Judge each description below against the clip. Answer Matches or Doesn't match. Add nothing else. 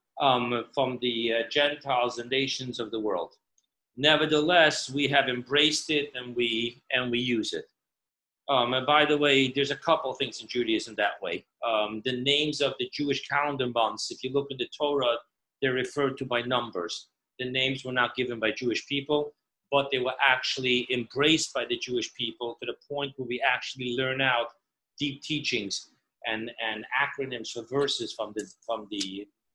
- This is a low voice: Matches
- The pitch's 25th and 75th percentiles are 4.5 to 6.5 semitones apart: Doesn't match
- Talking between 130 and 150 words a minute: Doesn't match